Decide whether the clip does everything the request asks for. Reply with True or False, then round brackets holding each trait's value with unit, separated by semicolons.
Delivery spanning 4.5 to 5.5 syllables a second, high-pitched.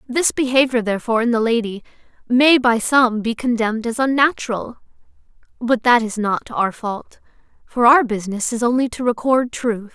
True (5.2 syllables/s; 235 Hz)